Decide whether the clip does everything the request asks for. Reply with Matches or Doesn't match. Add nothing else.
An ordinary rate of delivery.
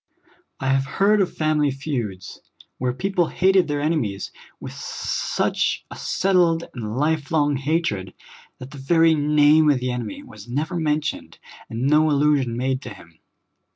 Matches